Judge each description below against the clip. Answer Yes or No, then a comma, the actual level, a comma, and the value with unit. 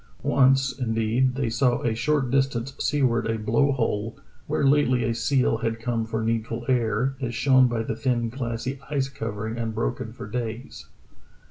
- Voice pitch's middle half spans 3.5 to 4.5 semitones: No, average, 2.7 semitones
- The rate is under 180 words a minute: Yes, average, 160 wpm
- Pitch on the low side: Yes, low, 120 Hz